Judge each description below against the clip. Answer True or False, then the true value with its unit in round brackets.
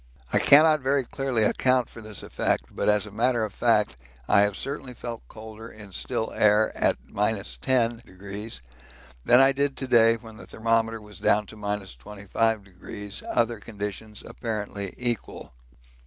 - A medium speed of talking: True (150 wpm)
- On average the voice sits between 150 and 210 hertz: False (110 Hz)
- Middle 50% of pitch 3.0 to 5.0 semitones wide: False (2.6 semitones)